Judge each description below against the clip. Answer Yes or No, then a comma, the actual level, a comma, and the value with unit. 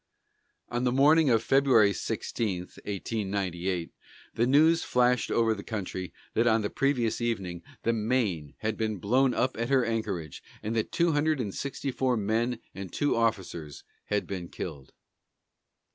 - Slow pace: No, average, 155 wpm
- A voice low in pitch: Yes, low, 115 Hz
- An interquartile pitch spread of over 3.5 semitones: Yes, average, 4.3 semitones